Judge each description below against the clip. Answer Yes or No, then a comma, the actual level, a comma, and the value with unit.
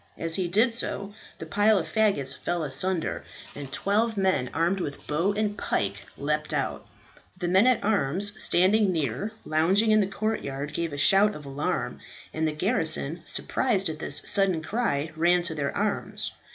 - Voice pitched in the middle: Yes, medium, 175 Hz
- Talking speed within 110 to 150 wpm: No, average, 170 wpm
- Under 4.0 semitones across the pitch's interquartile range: No, average, 5.2 semitones